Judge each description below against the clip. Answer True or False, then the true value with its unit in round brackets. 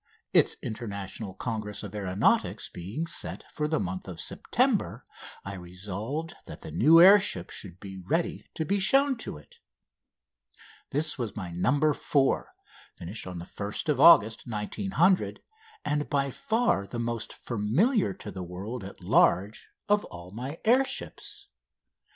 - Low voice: True (115 Hz)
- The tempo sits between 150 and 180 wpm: False (140 wpm)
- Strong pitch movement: True (8.5 semitones)